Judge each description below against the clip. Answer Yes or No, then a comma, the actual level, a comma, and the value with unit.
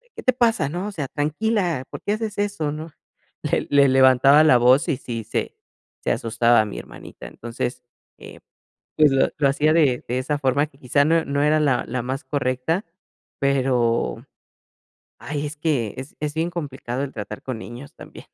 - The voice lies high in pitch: No, medium, 140 Hz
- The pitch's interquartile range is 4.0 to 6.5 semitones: No, average, 3.5 semitones